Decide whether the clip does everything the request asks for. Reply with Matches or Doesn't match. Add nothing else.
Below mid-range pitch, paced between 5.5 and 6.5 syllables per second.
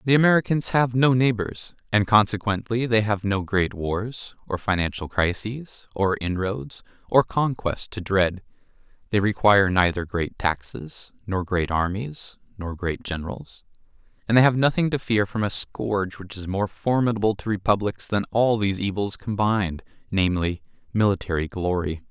Doesn't match